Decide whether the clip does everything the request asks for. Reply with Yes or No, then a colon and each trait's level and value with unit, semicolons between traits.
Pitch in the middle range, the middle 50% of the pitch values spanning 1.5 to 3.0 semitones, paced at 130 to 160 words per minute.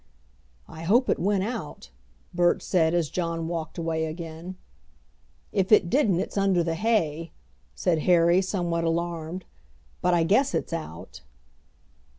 Yes: medium, 170 Hz; narrow, 2.4 semitones; average, 140 wpm